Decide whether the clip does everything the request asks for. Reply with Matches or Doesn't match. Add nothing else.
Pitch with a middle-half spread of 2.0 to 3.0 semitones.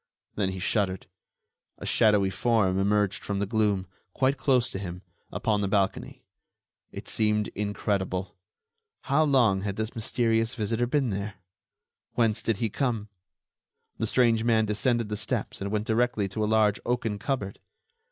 Matches